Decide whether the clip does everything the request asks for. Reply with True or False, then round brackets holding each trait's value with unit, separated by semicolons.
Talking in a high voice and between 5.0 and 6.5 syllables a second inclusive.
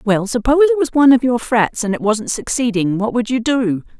True (235 Hz; 5.3 syllables/s)